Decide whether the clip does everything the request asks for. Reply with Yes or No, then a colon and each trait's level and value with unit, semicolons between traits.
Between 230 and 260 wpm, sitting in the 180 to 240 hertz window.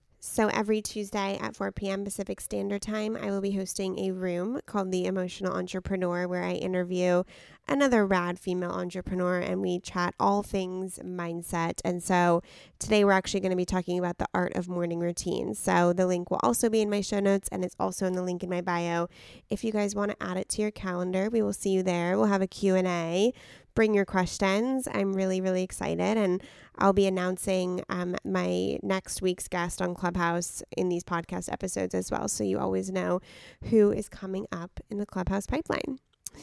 No: average, 200 wpm; medium, 185 Hz